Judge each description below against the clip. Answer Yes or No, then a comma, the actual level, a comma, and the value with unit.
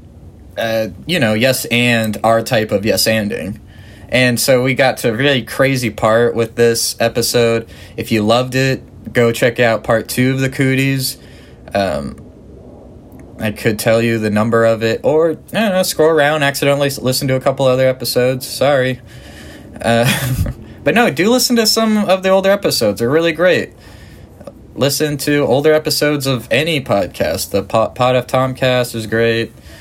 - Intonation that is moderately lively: Yes, average, 3.2 semitones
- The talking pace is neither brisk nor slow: Yes, average, 165 wpm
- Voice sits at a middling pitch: No, low, 120 Hz